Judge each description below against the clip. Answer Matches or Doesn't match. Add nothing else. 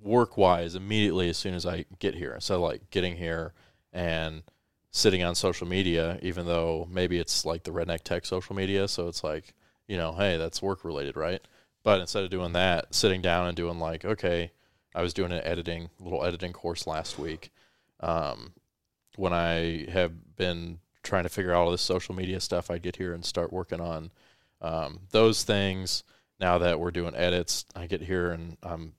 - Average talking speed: Matches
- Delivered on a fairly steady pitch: Matches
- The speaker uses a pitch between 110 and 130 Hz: Doesn't match